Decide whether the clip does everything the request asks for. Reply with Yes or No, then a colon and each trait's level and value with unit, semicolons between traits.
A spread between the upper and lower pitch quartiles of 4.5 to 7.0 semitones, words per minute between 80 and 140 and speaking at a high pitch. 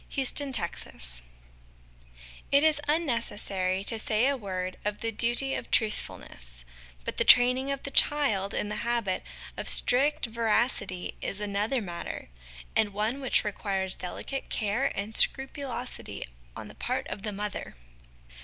Yes: average, 5.2 semitones; slow, 135 wpm; high, 220 Hz